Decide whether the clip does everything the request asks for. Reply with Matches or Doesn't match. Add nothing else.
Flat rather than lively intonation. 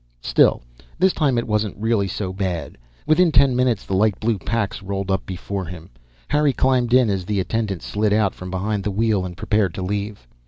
Doesn't match